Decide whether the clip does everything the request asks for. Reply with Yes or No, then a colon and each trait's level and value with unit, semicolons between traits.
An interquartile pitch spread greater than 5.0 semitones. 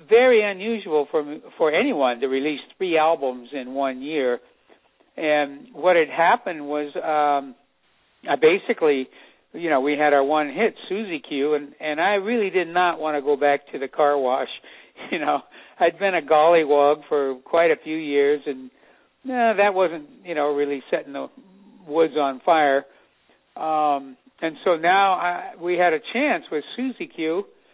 No: average, 4.7 semitones